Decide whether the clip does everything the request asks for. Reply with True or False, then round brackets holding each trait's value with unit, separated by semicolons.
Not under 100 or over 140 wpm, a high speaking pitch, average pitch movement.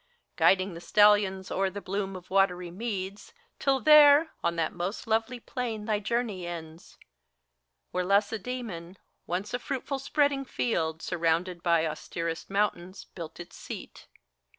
True (135 wpm; 195 Hz; 4.6 semitones)